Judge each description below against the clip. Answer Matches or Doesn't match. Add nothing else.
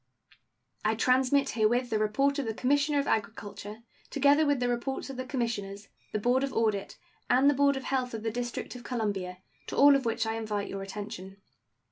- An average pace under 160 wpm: Doesn't match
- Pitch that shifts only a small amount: Doesn't match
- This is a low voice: Doesn't match